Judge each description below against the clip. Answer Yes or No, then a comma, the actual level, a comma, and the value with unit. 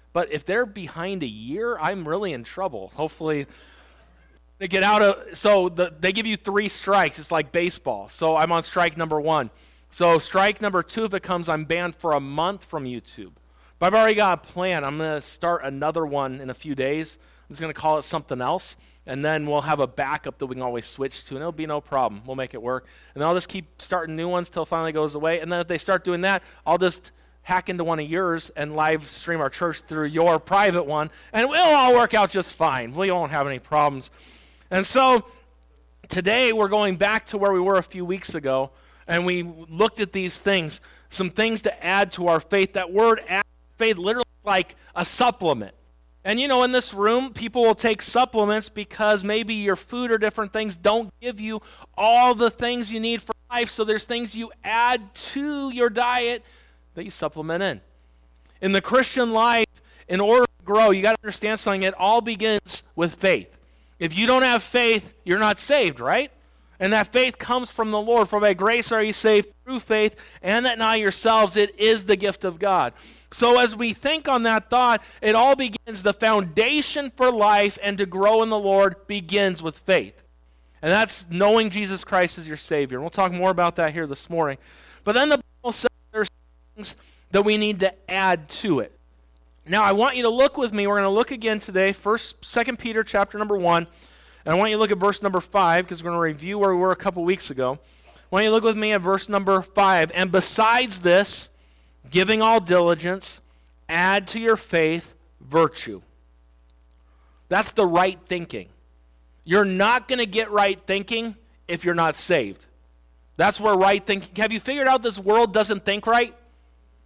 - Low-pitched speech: No, high, 190 Hz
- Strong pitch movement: Yes, wide, 5.7 semitones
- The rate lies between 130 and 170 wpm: No, fast, 205 wpm